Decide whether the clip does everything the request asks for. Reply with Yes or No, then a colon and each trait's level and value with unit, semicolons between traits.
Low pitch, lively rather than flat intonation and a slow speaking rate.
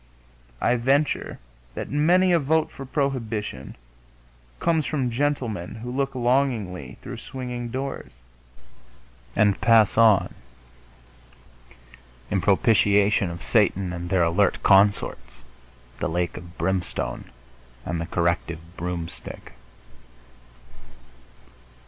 Yes: low, 105 Hz; wide, 7.0 semitones; slow, 100 wpm